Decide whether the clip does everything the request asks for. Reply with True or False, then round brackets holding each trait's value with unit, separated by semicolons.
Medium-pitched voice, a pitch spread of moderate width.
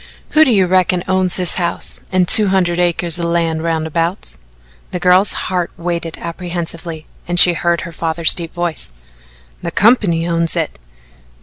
False (175 Hz; 1.6 semitones)